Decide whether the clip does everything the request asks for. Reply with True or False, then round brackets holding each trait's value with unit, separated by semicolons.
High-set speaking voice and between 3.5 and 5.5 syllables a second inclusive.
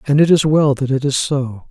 False (140 Hz; 5.2 syllables/s)